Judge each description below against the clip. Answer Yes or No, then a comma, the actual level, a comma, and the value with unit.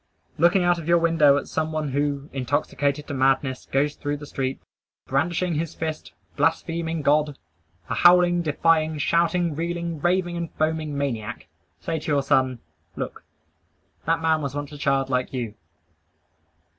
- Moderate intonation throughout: Yes, average, 3.0 semitones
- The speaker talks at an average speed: Yes, average, 155 wpm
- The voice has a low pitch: No, medium, 155 Hz